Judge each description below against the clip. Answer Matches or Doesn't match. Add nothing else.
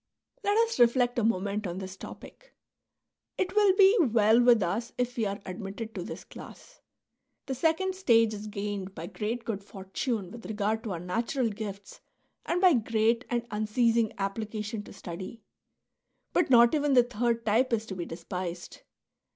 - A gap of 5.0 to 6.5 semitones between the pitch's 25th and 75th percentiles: Doesn't match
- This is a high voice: Matches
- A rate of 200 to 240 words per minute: Doesn't match